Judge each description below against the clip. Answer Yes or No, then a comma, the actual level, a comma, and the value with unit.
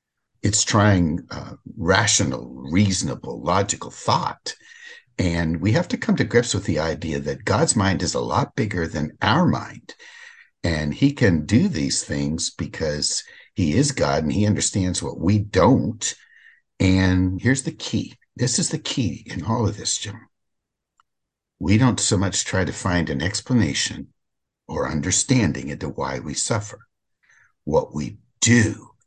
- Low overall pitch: Yes, low, 105 Hz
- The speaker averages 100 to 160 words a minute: Yes, average, 155 wpm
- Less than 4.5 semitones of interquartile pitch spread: No, wide, 5.4 semitones